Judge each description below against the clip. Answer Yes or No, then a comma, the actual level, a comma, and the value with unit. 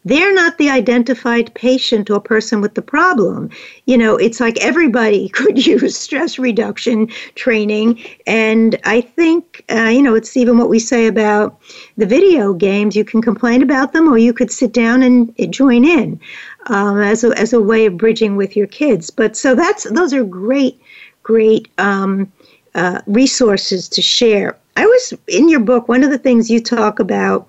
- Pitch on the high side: Yes, high, 235 Hz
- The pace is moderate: Yes, average, 185 wpm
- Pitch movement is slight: No, average, 3.1 semitones